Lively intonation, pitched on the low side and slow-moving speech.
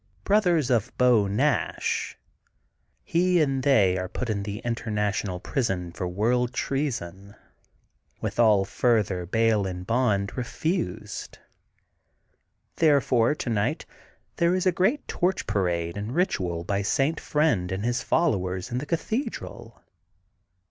Yes: wide, 6.8 semitones; low, 115 Hz; slow, 120 wpm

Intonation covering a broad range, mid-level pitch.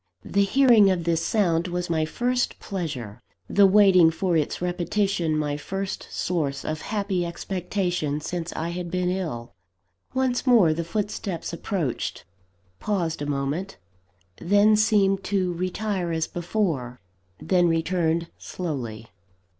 No: average, 3.5 semitones; medium, 175 Hz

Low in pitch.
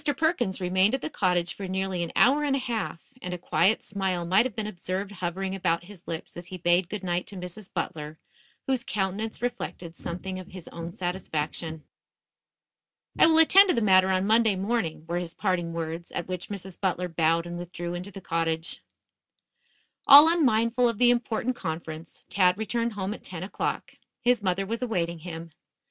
No: medium, 185 Hz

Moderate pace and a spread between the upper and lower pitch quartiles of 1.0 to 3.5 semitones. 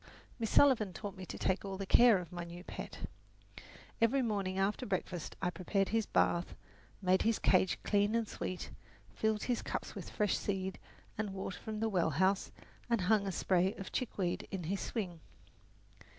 Yes: average, 180 wpm; average, 2.8 semitones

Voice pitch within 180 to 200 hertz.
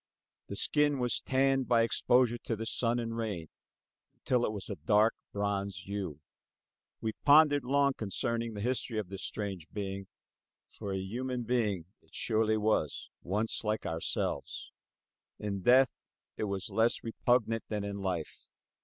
No: low, 110 Hz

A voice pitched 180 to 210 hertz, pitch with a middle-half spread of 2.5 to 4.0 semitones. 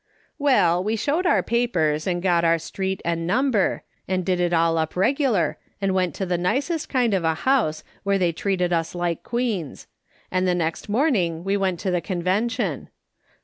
No: medium, 185 Hz; average, 4.7 semitones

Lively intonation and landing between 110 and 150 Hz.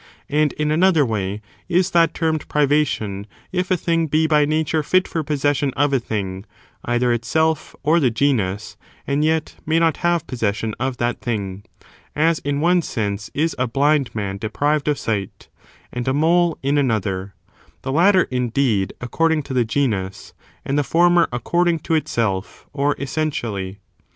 Yes: wide, 5.9 semitones; medium, 140 Hz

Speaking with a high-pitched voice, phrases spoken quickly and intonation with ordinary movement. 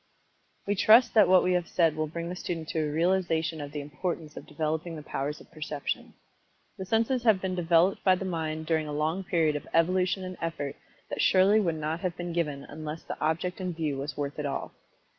No: medium, 165 Hz; fast, 215 wpm; average, 3.0 semitones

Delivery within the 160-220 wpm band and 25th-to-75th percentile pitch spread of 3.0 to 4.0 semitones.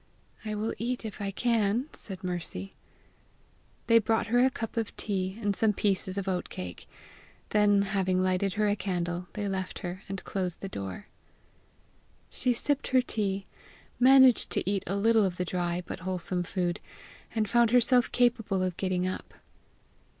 Yes: average, 165 wpm; average, 3.4 semitones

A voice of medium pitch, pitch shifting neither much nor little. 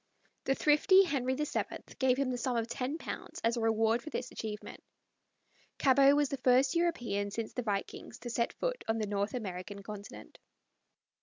No: high, 245 Hz; average, 3.9 semitones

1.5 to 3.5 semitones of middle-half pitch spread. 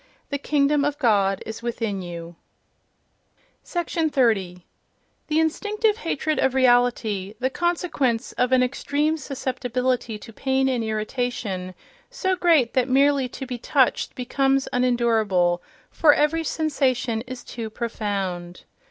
No: average, 4.6 semitones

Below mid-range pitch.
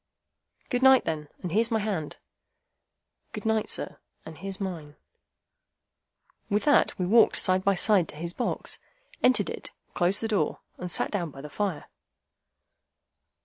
No: high, 195 Hz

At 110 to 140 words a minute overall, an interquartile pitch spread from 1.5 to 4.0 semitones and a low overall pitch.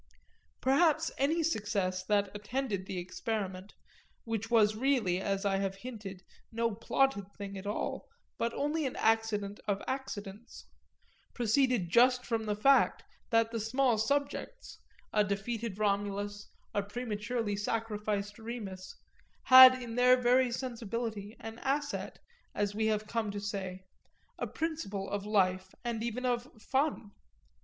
No: slow, 135 wpm; average, 3.6 semitones; high, 220 Hz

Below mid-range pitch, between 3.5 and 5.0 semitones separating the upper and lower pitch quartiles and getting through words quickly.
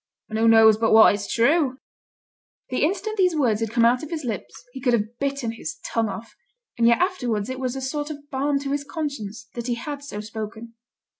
No: high, 245 Hz; average, 4.2 semitones; fast, 220 wpm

